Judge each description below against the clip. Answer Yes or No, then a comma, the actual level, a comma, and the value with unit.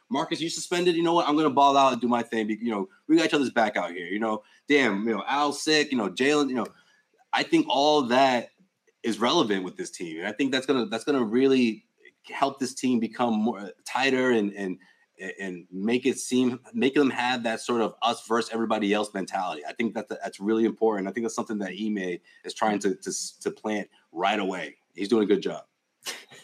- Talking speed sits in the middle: No, fast, 225 wpm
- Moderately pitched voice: No, low, 120 Hz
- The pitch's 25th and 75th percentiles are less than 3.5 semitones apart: No, average, 4.7 semitones